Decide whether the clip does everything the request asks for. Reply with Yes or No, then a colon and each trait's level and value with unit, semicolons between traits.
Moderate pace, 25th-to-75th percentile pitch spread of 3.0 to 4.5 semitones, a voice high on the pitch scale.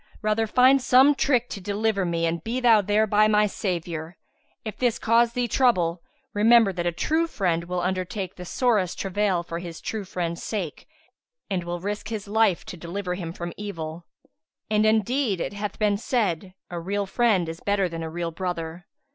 Yes: average, 180 wpm; average, 4.1 semitones; high, 195 Hz